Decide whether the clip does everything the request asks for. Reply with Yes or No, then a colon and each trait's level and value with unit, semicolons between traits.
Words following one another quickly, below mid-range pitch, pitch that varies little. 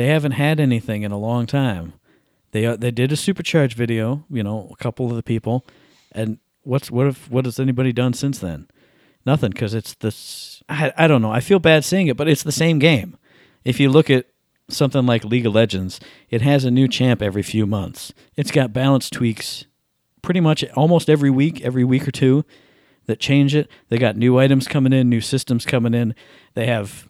No: fast, 210 wpm; low, 130 Hz; average, 3.5 semitones